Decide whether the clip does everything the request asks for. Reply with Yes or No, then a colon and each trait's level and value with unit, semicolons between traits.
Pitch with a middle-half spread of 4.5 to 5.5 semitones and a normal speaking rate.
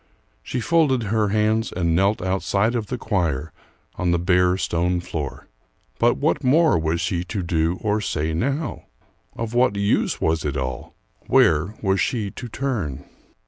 Yes: average, 5.0 semitones; average, 160 wpm